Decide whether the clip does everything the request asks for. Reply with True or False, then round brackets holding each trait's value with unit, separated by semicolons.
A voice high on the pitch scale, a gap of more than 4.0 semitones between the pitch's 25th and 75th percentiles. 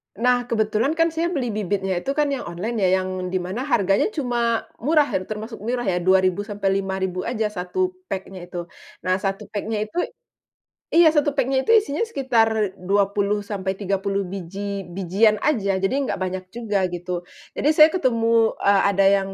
True (205 Hz; 4.4 semitones)